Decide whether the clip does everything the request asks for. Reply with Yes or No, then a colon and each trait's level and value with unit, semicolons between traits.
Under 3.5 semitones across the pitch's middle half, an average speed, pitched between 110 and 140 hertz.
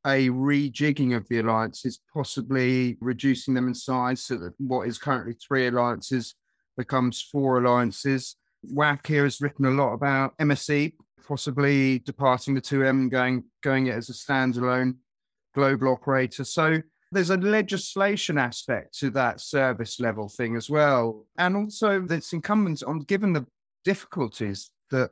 Yes: narrow, 2.5 semitones; average, 150 wpm; low, 135 Hz